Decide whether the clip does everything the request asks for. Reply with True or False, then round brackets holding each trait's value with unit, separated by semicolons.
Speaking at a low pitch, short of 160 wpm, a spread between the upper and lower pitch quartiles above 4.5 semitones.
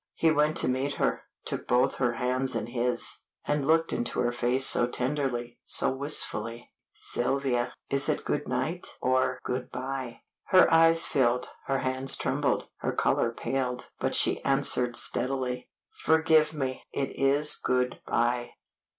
False (130 Hz; 150 wpm; 2.5 semitones)